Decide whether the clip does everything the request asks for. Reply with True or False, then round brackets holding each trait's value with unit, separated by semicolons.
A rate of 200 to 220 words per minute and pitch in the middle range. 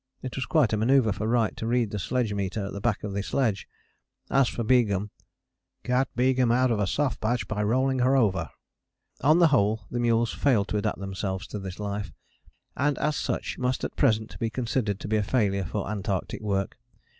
False (205 wpm; 110 Hz)